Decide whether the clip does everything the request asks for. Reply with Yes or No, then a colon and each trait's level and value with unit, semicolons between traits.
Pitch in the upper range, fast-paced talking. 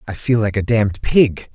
No: low, 110 Hz; fast, 235 wpm